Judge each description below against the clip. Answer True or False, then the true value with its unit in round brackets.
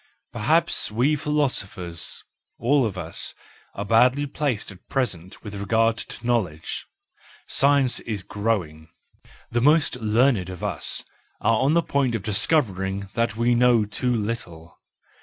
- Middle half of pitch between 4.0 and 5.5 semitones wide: True (4.6 semitones)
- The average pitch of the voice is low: True (115 Hz)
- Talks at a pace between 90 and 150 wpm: True (135 wpm)